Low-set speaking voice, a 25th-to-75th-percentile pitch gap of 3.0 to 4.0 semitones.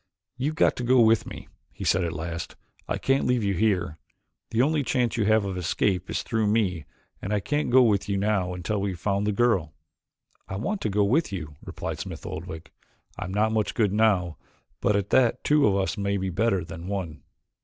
Yes: low, 100 Hz; average, 3.6 semitones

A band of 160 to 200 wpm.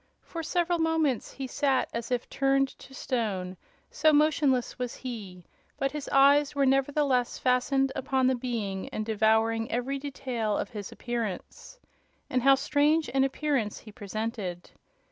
No: average, 145 wpm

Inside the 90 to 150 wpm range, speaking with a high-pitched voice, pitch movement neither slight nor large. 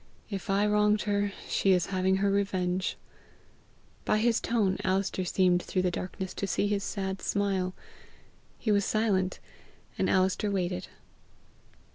No: average, 140 wpm; high, 195 Hz; narrow, 1.6 semitones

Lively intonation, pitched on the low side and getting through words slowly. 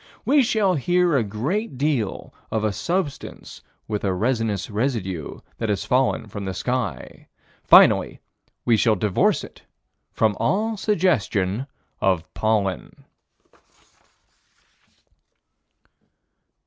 Yes: wide, 7.3 semitones; low, 115 Hz; slow, 105 wpm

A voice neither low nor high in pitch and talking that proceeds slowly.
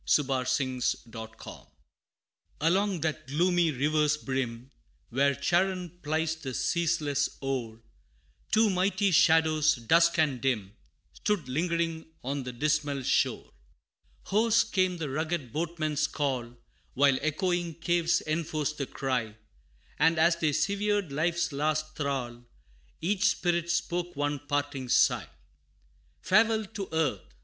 Yes: medium, 155 Hz; slow, 120 wpm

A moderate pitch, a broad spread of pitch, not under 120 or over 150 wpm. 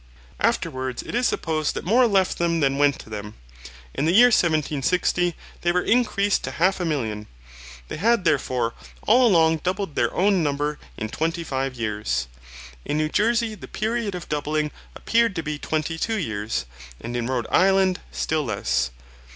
No: medium, 160 Hz; wide, 6.3 semitones; average, 170 wpm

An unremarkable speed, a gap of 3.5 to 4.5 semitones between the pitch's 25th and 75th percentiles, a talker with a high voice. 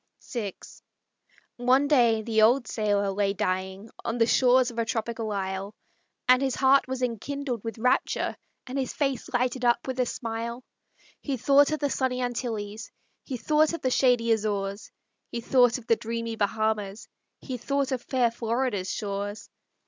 No: average, 165 wpm; average, 3.0 semitones; high, 235 Hz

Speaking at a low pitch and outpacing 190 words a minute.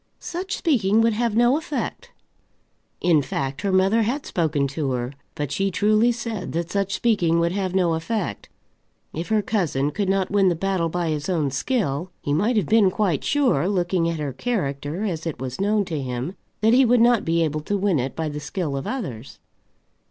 No: medium, 185 Hz; average, 200 wpm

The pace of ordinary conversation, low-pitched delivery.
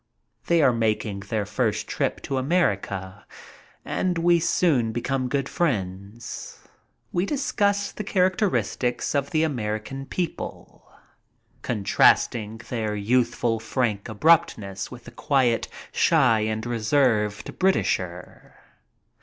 No: slow, 105 wpm; low, 120 Hz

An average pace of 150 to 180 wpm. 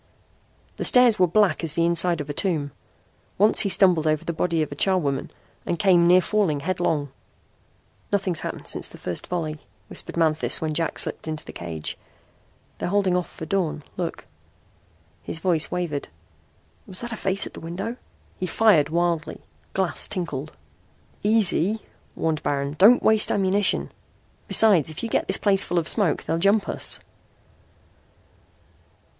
Yes: average, 160 wpm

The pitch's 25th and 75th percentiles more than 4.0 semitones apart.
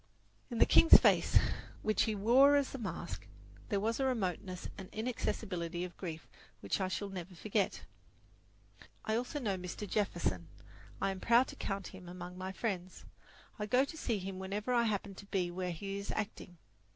No: average, 3.5 semitones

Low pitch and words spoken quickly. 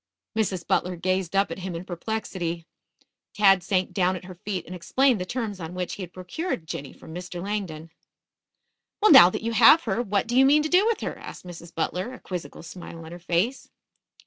No: medium, 185 Hz; fast, 210 wpm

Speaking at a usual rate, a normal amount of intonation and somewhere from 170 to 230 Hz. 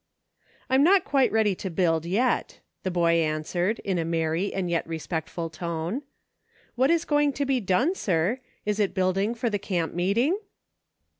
No: average, 170 wpm; wide, 6.6 semitones; high, 190 Hz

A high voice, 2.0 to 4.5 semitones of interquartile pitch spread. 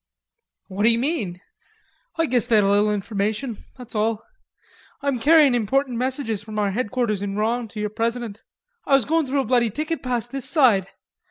Yes: high, 235 Hz; average, 3.9 semitones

